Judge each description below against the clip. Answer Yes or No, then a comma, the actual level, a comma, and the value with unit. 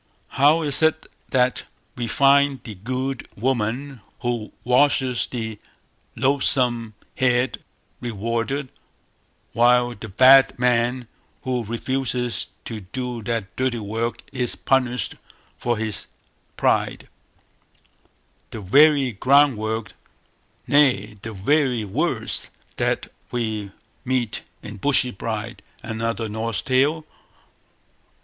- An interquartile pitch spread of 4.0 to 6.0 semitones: No, average, 2.9 semitones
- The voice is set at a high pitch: No, low, 120 Hz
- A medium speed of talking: No, slow, 100 wpm